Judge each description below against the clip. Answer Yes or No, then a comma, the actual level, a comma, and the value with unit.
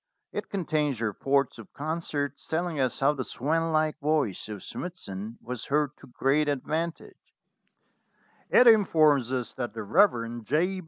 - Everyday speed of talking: Yes, average, 145 wpm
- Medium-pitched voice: Yes, medium, 145 Hz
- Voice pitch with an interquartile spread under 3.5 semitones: No, average, 4.7 semitones